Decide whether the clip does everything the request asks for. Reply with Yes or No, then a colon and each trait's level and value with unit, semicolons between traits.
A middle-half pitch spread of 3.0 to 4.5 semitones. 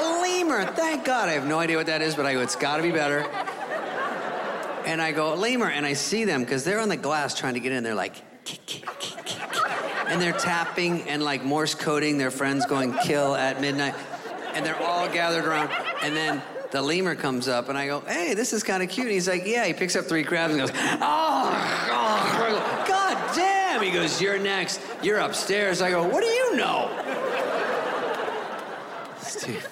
No: wide, 5.4 semitones